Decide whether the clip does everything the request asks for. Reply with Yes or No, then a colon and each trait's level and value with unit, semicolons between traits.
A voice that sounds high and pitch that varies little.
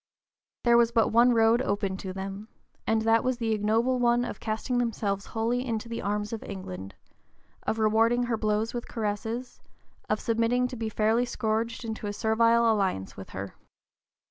Yes: high, 225 Hz; narrow, 2.1 semitones